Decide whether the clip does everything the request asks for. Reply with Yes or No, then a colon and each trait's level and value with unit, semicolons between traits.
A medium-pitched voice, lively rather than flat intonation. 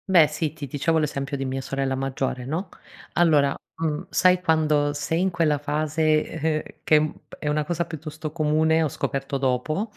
No: medium, 150 Hz; narrow, 2.4 semitones